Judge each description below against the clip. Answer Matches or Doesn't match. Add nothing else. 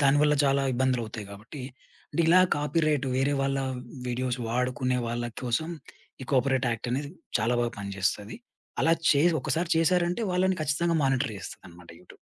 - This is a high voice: Doesn't match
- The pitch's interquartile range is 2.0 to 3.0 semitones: Doesn't match